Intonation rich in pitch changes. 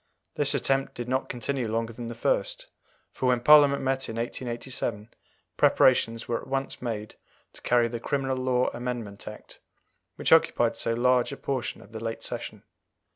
No: narrow, 2.5 semitones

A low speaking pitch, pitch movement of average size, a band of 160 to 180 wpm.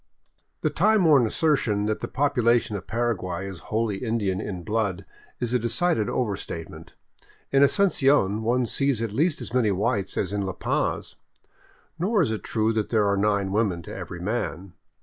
Yes: low, 110 Hz; average, 4.3 semitones; average, 170 wpm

